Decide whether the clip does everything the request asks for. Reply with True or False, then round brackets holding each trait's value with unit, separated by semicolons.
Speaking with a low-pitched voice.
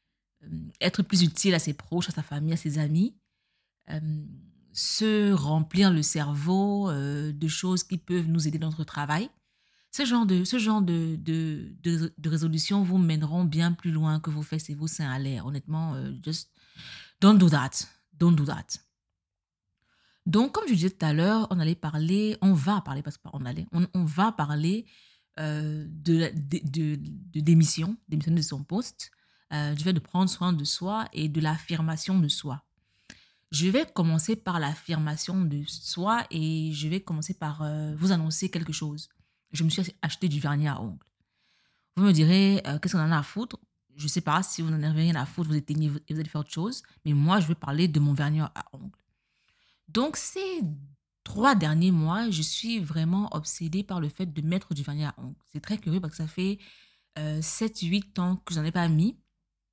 False (165 Hz)